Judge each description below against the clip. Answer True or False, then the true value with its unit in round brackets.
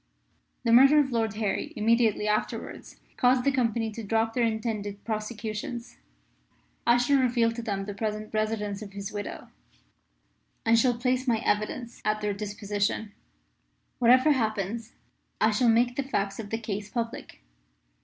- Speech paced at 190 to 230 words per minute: False (150 wpm)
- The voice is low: False (225 Hz)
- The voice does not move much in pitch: True (2.3 semitones)